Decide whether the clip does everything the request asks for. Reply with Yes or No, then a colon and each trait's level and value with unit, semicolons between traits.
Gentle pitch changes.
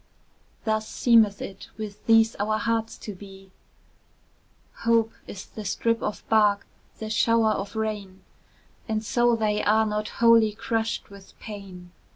Yes: narrow, 1.8 semitones